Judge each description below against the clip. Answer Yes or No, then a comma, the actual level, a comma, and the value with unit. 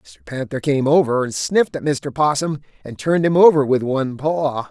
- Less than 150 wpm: No, fast, 205 wpm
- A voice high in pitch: No, medium, 140 Hz